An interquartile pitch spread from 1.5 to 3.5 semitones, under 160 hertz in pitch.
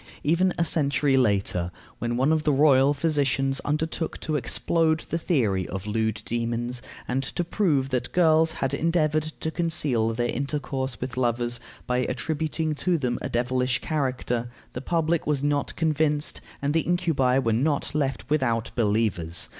No: average, 4.5 semitones; low, 135 Hz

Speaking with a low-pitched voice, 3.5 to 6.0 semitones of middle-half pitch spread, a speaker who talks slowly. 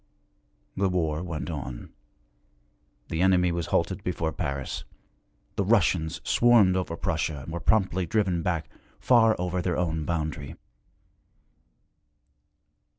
No: very low, 85 Hz; average, 2.8 semitones; slow, 115 wpm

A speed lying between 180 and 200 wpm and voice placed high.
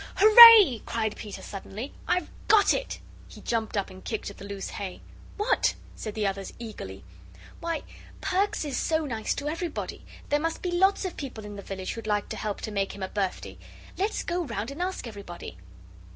Yes: average, 195 wpm; high, 230 Hz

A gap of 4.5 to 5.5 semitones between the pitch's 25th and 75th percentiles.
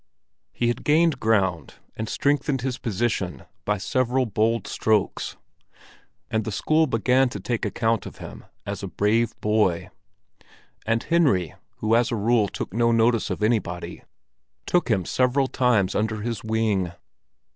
No: average, 3.0 semitones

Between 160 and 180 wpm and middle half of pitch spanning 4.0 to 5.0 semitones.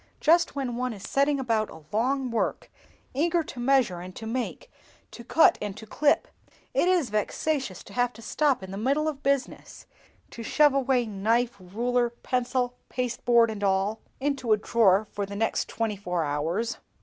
Yes: average, 175 wpm; average, 4.6 semitones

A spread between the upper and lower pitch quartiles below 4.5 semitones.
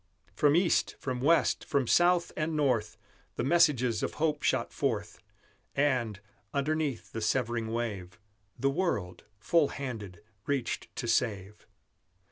No: average, 5.3 semitones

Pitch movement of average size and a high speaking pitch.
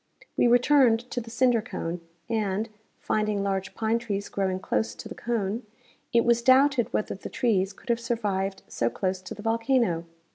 Yes: average, 3.5 semitones; high, 220 Hz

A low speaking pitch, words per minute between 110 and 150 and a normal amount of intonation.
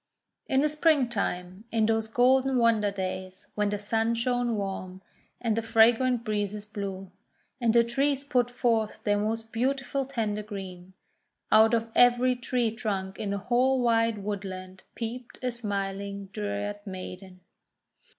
No: high, 220 Hz; average, 145 wpm; average, 3.3 semitones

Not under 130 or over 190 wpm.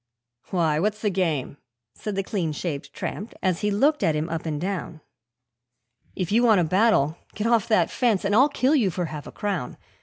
No: fast, 205 wpm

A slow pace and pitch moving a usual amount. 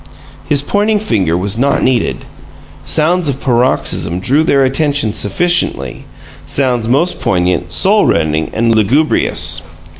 No: slow, 120 wpm; wide, 8.4 semitones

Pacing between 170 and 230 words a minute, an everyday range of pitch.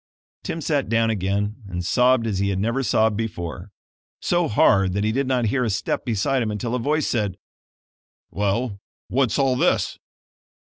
Yes: average, 175 wpm; average, 4.2 semitones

